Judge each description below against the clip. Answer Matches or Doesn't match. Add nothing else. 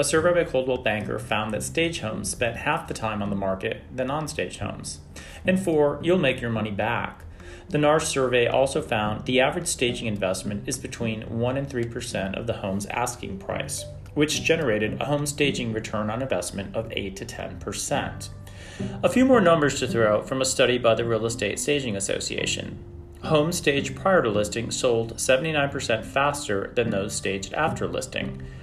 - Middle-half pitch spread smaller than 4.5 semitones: Doesn't match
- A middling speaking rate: Matches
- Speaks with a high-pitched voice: Doesn't match